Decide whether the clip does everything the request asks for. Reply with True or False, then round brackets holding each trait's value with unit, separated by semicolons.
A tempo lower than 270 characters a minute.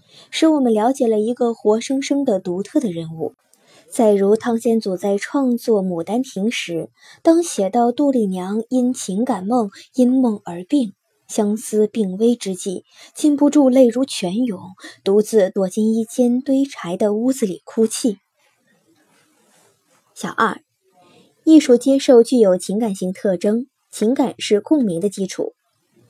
True (210 characters per minute)